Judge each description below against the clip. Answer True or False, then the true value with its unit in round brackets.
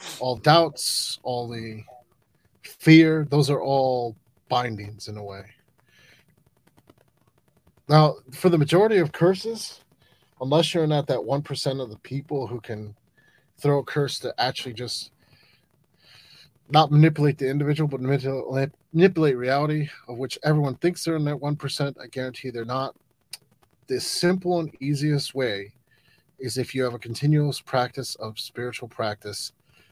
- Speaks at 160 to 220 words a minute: False (140 wpm)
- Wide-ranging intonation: False (3.3 semitones)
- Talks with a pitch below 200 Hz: True (135 Hz)